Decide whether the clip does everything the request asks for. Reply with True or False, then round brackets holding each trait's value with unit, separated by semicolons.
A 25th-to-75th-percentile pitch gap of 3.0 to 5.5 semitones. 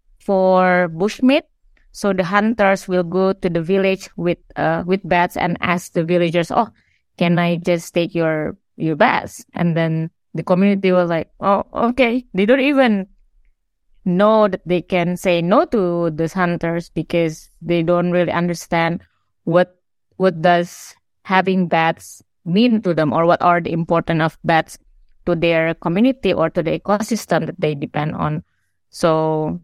False (2.5 semitones)